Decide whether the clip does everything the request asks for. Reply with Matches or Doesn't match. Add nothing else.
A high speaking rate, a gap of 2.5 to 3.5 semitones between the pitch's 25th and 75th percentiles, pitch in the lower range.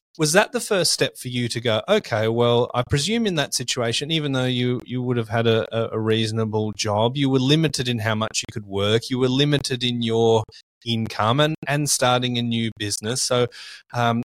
Matches